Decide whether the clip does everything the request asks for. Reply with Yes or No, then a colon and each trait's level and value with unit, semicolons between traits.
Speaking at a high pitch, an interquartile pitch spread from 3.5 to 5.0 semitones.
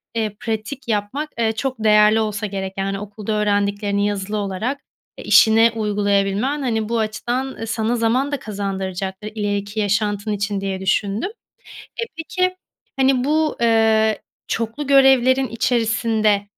No: high, 215 Hz; average, 3.1 semitones